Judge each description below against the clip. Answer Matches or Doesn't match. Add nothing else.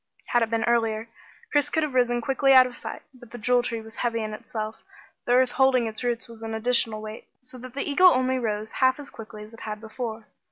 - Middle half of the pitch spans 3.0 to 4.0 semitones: Doesn't match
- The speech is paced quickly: Matches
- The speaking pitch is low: Doesn't match